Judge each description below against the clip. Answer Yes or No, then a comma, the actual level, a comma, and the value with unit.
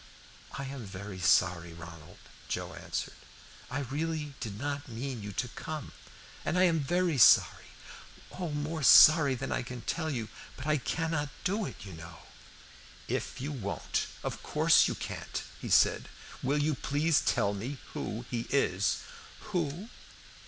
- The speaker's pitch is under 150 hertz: Yes, medium, 140 Hz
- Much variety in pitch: Yes, wide, 6.6 semitones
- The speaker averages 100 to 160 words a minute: Yes, average, 155 wpm